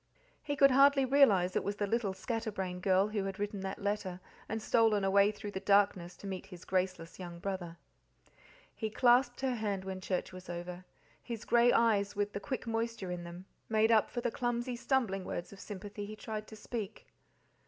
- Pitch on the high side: Yes, high, 205 Hz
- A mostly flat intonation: No, average, 3.3 semitones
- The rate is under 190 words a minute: No, average, 195 wpm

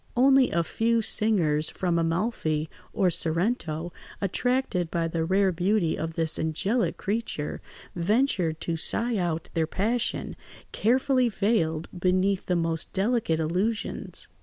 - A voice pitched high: No, medium, 180 Hz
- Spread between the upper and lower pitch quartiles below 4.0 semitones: No, wide, 5.4 semitones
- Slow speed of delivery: Yes, slow, 125 wpm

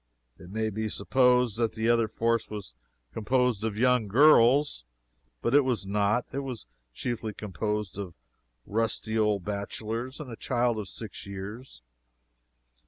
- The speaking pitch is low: Yes, low, 110 Hz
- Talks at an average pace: Yes, average, 145 wpm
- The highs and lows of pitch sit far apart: No, average, 3.1 semitones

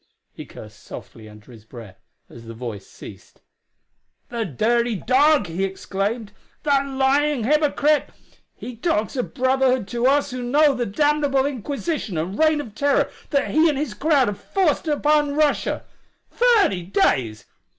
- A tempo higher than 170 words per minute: No, average, 150 wpm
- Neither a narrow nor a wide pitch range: No, wide, 6.8 semitones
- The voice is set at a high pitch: Yes, very high, 260 Hz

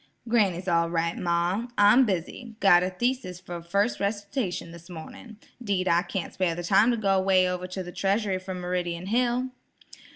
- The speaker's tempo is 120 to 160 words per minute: No, average, 175 wpm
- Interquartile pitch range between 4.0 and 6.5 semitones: No, average, 2.9 semitones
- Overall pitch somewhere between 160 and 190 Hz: Yes, medium, 185 Hz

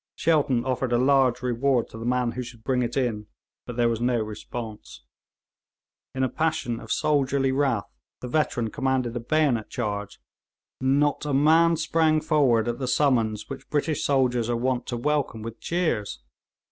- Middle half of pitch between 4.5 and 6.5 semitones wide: No, average, 3.3 semitones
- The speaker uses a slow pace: No, average, 170 wpm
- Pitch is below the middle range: Yes, low, 125 Hz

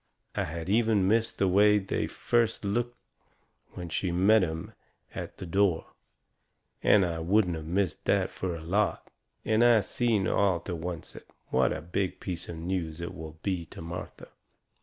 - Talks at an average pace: Yes, average, 170 wpm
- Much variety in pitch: No, average, 3.6 semitones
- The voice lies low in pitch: Yes, very low, 95 Hz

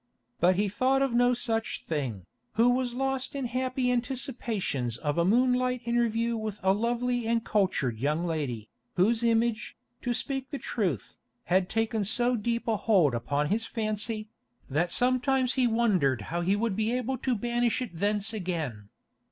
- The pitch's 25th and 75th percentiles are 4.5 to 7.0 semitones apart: Yes, average, 5.2 semitones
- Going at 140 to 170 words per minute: Yes, average, 160 wpm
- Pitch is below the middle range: No, high, 225 Hz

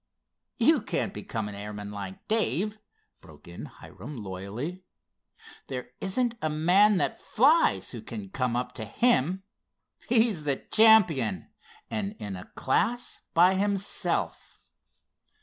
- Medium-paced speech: No, slow, 125 wpm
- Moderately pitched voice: Yes, medium, 170 Hz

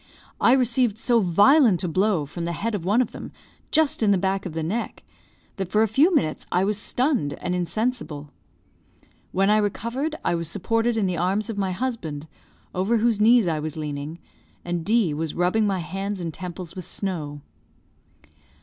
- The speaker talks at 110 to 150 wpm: No, average, 185 wpm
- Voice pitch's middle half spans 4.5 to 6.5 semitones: Yes, average, 4.9 semitones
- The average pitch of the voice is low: No, high, 195 Hz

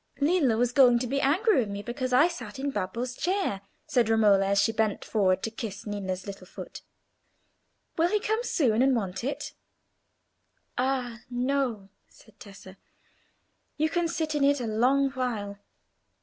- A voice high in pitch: Yes, high, 245 Hz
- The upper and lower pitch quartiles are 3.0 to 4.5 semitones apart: No, average, 5.1 semitones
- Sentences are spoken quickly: No, average, 165 wpm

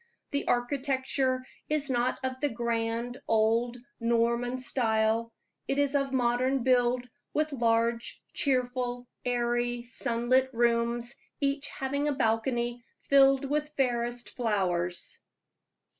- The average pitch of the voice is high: Yes, high, 245 Hz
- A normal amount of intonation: No, narrow, 2.1 semitones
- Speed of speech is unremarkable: No, slow, 110 wpm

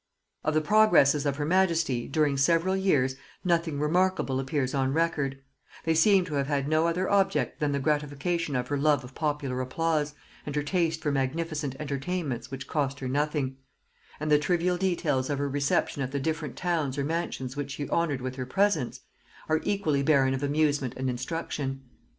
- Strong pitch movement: No, average, 3.4 semitones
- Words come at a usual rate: Yes, average, 180 wpm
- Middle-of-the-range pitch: Yes, medium, 150 Hz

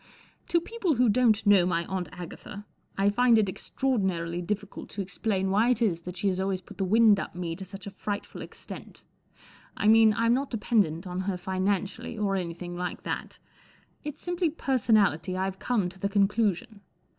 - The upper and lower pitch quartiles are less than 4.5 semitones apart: Yes, average, 3.6 semitones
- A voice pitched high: Yes, high, 200 Hz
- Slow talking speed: No, average, 200 wpm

